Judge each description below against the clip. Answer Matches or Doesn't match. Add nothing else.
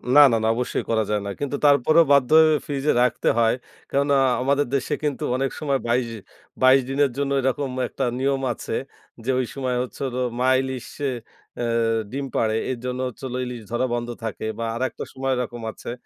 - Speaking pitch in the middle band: Doesn't match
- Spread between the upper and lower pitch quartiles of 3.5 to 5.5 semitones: Doesn't match